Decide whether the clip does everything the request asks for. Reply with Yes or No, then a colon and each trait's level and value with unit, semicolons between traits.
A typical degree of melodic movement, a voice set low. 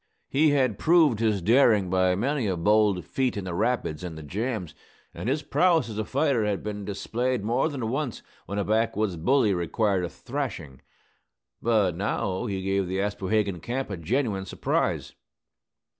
Yes: average, 4.9 semitones; low, 105 Hz